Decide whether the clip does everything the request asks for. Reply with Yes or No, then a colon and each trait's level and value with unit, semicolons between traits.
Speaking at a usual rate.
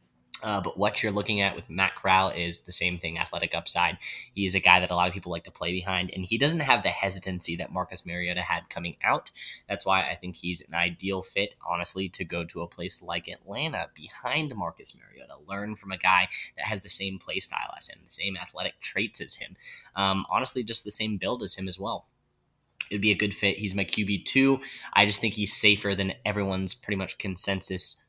No: fast, 225 wpm